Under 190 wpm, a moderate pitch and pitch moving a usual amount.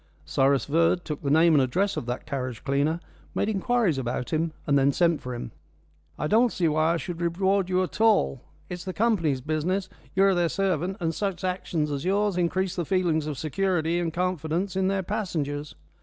No: average, 195 wpm; medium, 170 Hz; average, 4.0 semitones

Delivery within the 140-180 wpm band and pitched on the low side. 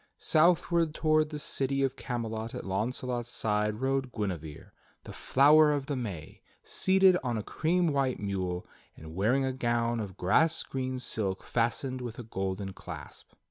Yes: average, 155 wpm; low, 125 Hz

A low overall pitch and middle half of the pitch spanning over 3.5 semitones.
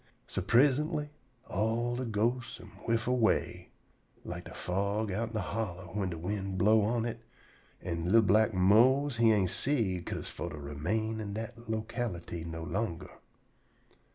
Yes: low, 110 Hz; average, 4.0 semitones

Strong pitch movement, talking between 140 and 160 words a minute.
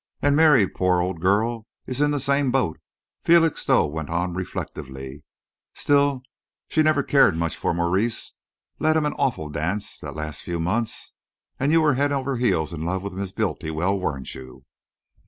No: wide, 9.0 semitones; average, 170 wpm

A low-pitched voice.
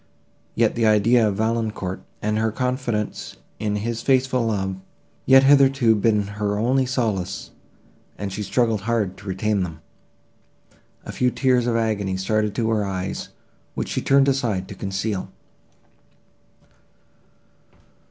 Yes: low, 110 Hz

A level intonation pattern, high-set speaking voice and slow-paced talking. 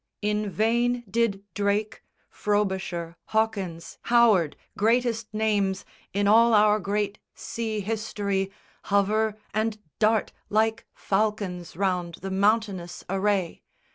Yes: narrow, 2.1 semitones; high, 210 Hz; slow, 105 wpm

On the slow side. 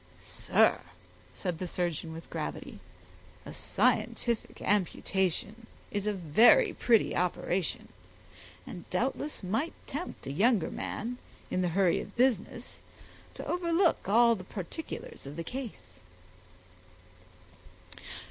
Yes: slow, 110 wpm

